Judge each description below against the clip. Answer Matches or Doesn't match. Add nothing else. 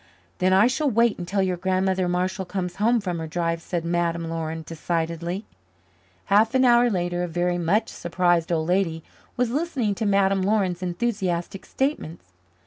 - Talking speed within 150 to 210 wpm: Matches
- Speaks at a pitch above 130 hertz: Matches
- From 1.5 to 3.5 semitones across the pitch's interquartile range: Matches